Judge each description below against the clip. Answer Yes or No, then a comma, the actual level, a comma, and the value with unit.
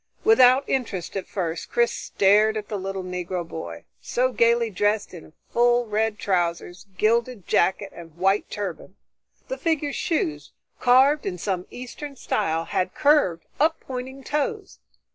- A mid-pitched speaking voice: No, high, 210 Hz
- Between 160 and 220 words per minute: No, average, 145 wpm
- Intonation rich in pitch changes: Yes, wide, 5.7 semitones